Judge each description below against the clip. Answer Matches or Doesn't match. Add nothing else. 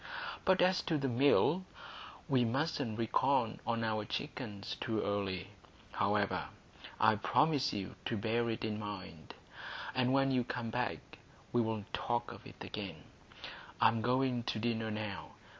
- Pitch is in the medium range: Doesn't match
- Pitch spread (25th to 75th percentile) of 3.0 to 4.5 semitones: Matches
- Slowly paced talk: Doesn't match